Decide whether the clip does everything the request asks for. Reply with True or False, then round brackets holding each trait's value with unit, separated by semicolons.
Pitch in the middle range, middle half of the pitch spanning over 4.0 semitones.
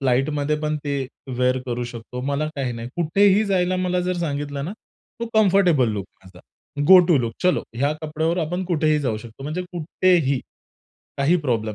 True (150 Hz; 5.5 semitones)